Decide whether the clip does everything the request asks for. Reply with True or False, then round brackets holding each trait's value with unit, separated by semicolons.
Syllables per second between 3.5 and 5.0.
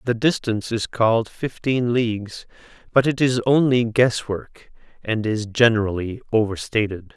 True (4.6 syllables/s)